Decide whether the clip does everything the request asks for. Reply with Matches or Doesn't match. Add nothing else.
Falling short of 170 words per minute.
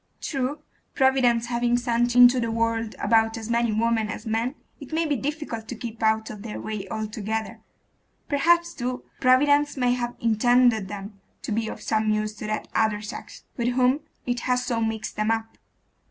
Doesn't match